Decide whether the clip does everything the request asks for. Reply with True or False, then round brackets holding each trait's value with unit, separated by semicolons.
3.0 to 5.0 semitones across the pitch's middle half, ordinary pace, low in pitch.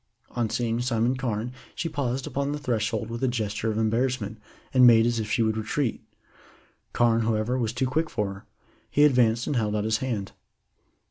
False (2.5 semitones; 190 wpm; 115 Hz)